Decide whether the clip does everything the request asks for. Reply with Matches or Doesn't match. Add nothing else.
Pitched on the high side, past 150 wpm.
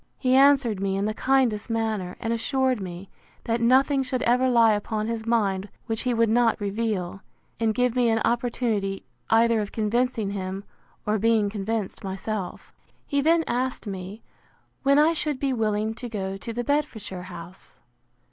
Matches